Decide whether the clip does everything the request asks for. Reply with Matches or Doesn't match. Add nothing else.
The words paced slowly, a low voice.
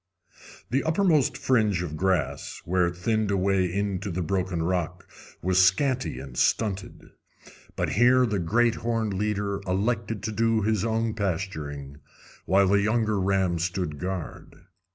Doesn't match